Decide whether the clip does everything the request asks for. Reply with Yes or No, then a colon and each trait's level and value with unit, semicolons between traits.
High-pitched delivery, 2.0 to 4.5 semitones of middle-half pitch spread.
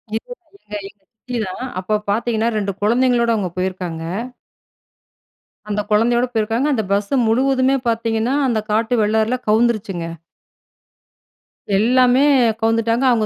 Yes: high, 225 Hz; narrow, 2.5 semitones